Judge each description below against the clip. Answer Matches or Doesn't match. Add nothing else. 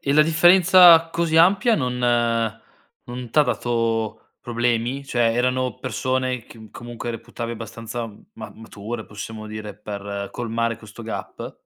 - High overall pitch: Doesn't match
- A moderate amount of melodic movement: Matches